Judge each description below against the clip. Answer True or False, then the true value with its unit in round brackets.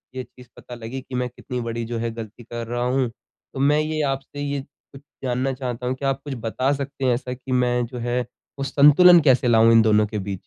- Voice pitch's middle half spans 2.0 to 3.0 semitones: True (2.6 semitones)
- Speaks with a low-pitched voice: True (125 Hz)